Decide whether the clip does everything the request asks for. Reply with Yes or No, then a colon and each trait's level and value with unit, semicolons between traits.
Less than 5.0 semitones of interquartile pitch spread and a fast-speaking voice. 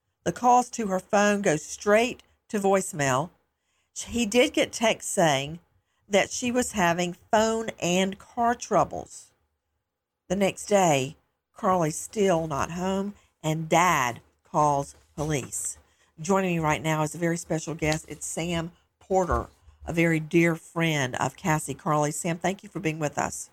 No: average, 4.4 semitones; average, 150 wpm